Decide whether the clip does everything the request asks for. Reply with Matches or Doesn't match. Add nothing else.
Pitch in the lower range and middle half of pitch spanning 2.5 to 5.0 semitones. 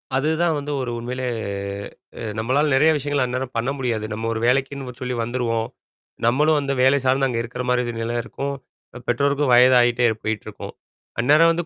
Matches